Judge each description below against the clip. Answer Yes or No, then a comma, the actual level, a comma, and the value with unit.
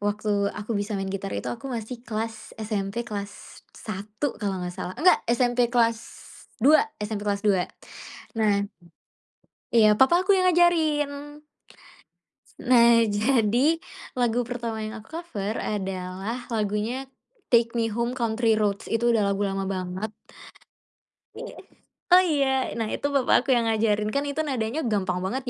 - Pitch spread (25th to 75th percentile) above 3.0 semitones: Yes, average, 3.6 semitones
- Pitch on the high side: Yes, high, 225 Hz